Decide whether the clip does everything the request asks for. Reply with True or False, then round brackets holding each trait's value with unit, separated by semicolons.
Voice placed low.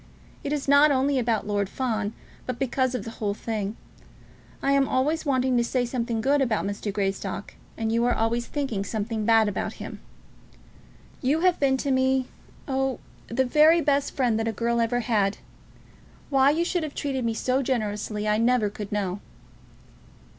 False (245 Hz)